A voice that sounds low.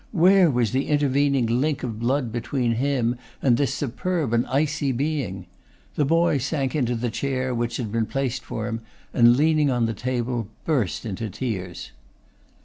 Yes: low, 130 Hz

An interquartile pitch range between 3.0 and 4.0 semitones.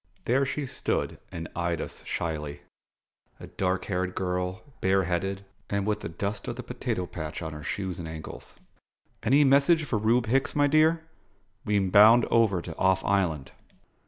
No: average, 5.0 semitones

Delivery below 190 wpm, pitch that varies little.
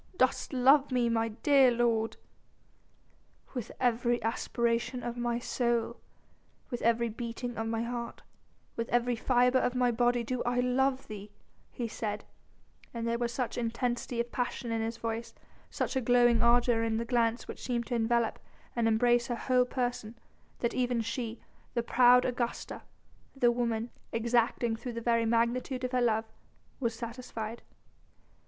Yes: average, 155 wpm; narrow, 1.3 semitones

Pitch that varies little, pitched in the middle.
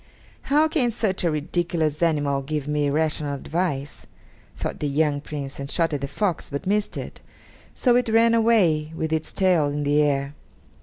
No: average, 4.5 semitones; medium, 155 Hz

